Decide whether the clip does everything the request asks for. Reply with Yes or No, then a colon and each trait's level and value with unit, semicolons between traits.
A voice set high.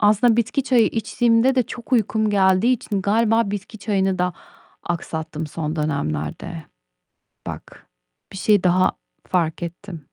Yes: high, 200 Hz